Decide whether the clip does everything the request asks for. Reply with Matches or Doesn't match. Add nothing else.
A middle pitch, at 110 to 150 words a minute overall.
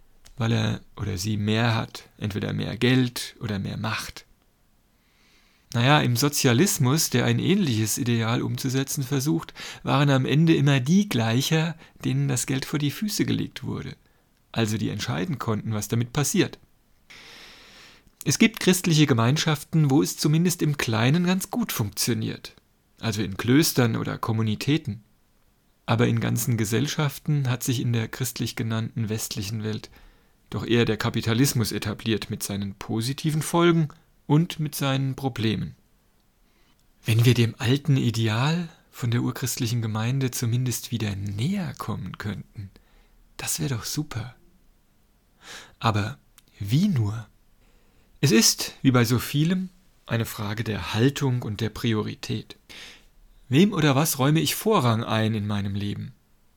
Doesn't match